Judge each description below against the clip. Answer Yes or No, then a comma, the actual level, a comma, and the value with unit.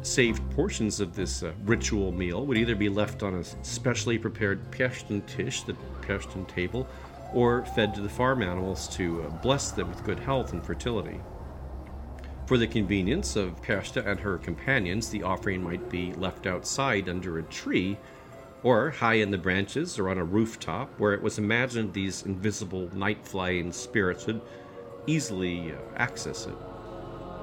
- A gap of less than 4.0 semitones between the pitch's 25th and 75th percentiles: No, average, 4.5 semitones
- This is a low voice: Yes, low, 100 Hz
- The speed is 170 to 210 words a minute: No, average, 160 wpm